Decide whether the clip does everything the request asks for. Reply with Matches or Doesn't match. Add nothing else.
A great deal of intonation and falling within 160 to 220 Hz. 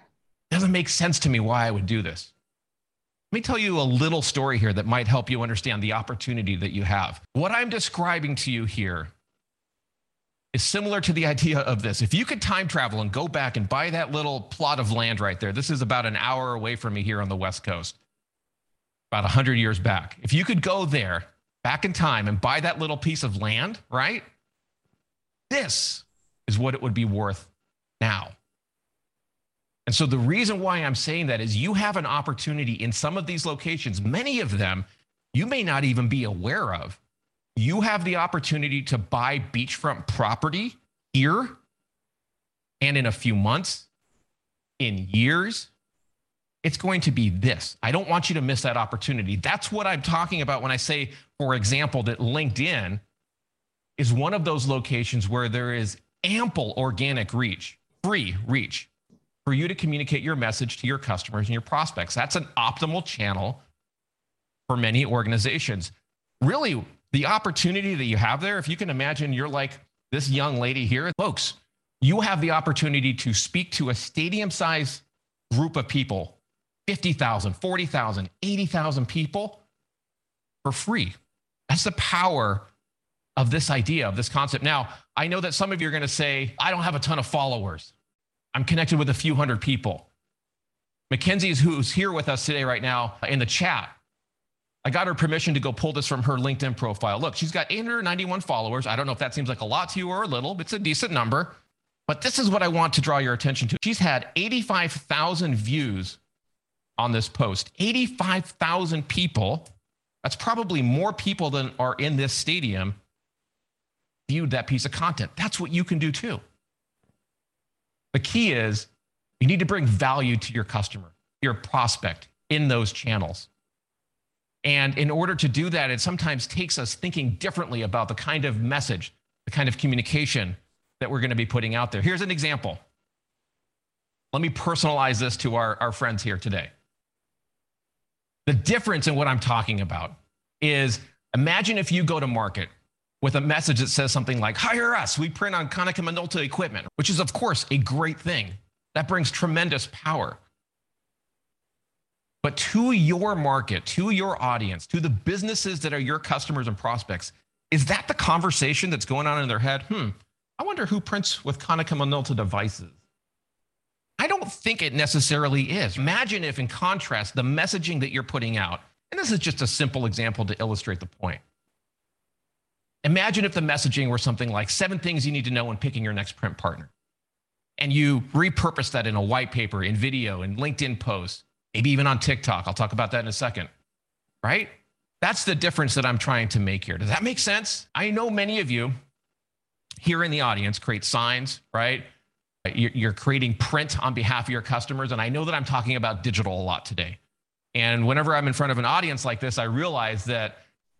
Doesn't match